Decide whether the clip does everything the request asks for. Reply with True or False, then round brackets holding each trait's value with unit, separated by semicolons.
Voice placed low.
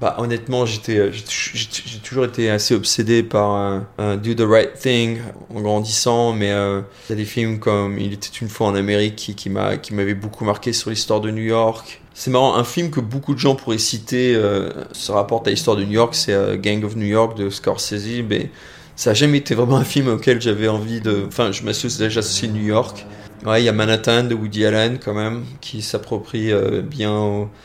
True (110 Hz)